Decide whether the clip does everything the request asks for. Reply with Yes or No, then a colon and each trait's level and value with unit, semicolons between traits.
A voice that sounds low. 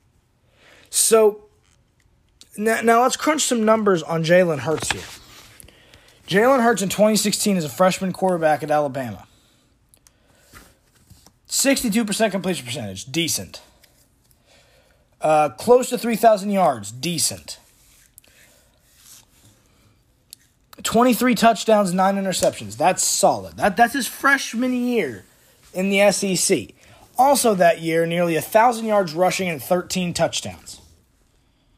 No: medium, 185 Hz